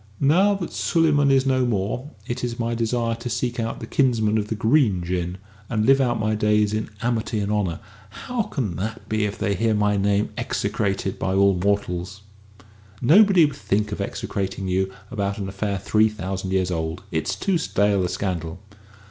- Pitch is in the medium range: No, low, 105 Hz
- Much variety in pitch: No, average, 3.9 semitones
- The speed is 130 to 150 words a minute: No, average, 185 wpm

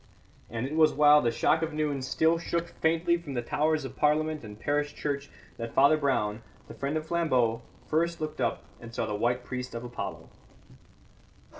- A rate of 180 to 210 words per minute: Yes, average, 185 wpm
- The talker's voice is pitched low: No, medium, 145 Hz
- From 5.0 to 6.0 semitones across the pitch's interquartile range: No, average, 4.3 semitones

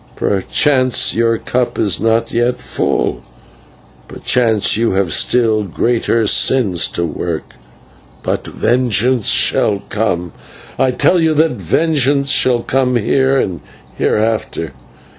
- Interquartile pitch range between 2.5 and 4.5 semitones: Yes, average, 4.1 semitones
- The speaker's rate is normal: No, slow, 115 wpm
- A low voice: Yes, low, 115 Hz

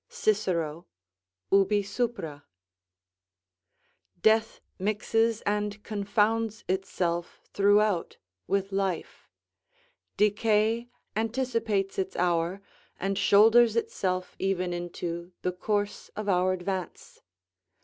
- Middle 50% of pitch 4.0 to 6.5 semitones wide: No, average, 2.9 semitones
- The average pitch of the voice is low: No, high, 200 Hz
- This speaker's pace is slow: Yes, slow, 85 wpm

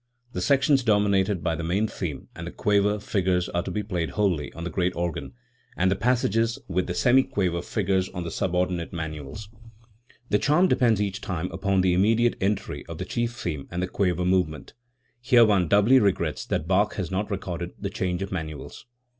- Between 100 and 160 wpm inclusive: No, average, 195 wpm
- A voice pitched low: Yes, very low, 95 Hz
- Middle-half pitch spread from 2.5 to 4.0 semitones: Yes, average, 3.0 semitones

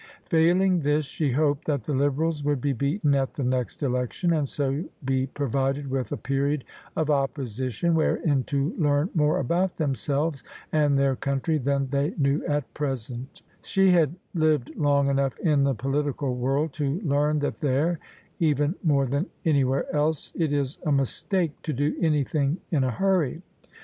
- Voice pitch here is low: No, medium, 145 Hz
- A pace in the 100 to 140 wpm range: No, average, 170 wpm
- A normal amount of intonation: No, narrow, 2.3 semitones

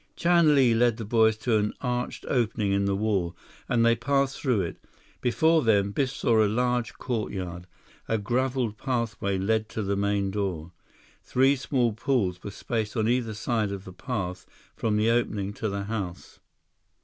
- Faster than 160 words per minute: Yes, average, 175 wpm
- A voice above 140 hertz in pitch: No, low, 110 Hz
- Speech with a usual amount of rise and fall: Yes, average, 3.5 semitones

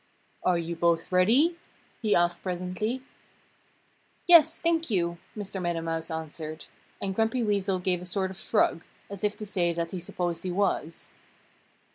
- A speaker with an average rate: Yes, average, 155 wpm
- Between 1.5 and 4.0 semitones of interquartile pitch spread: Yes, average, 3.5 semitones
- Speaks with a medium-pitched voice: Yes, medium, 180 Hz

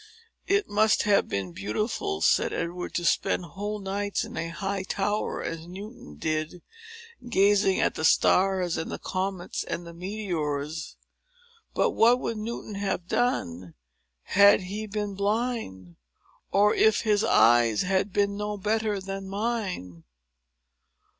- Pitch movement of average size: Yes, average, 3.9 semitones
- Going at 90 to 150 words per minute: Yes, slow, 135 wpm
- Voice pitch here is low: No, high, 195 Hz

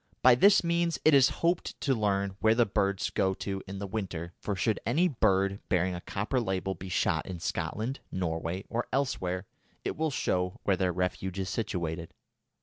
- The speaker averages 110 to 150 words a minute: No, average, 185 wpm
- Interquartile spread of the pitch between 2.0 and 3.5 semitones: No, average, 4.7 semitones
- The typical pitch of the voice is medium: No, low, 100 Hz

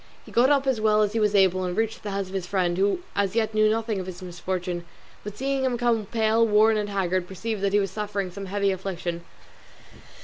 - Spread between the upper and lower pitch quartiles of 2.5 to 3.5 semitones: Yes, average, 2.8 semitones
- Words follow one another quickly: Yes, fast, 235 wpm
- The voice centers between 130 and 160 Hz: No, high, 205 Hz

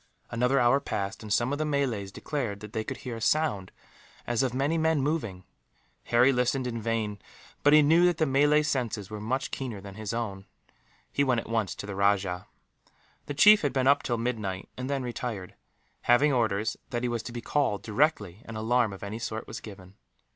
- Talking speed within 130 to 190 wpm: No, fast, 205 wpm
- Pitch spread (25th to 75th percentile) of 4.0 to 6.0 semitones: Yes, average, 4.7 semitones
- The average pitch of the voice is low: Yes, low, 120 Hz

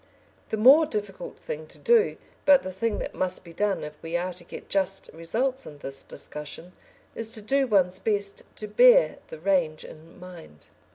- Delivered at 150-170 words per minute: No, average, 185 wpm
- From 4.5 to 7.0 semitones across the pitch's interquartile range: Yes, average, 5.3 semitones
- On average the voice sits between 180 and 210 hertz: Yes, high, 190 Hz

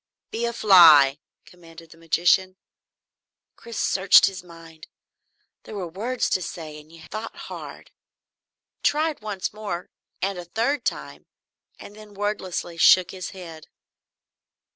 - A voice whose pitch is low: No, medium, 185 Hz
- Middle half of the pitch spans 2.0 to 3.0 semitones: No, average, 4.0 semitones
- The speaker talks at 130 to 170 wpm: Yes, slow, 135 wpm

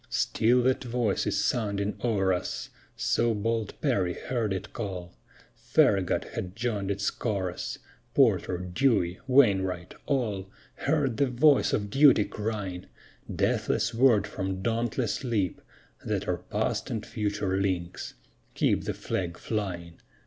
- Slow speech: Yes, slow, 130 wpm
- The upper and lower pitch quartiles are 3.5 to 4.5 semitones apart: Yes, average, 4.0 semitones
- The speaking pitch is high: No, low, 105 Hz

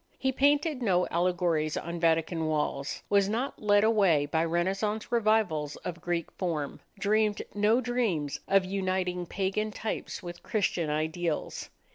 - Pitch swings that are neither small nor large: Yes, average, 4.4 semitones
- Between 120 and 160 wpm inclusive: Yes, slow, 135 wpm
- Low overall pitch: No, medium, 185 Hz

